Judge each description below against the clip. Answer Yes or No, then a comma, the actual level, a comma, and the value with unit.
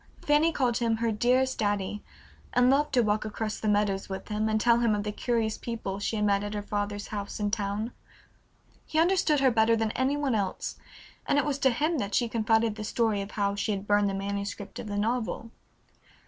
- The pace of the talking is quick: Yes, fast, 220 wpm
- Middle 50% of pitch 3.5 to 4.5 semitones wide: No, average, 2.8 semitones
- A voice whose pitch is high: Yes, high, 220 Hz